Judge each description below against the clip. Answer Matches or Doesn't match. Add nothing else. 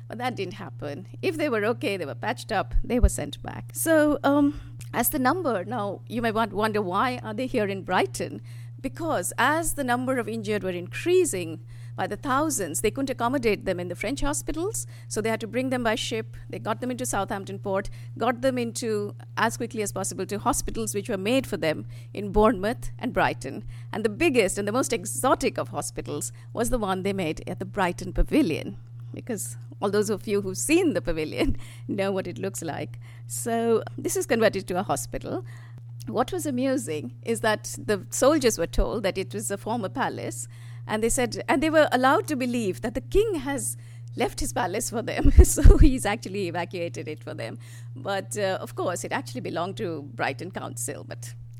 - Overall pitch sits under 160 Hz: Doesn't match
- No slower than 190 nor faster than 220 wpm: Matches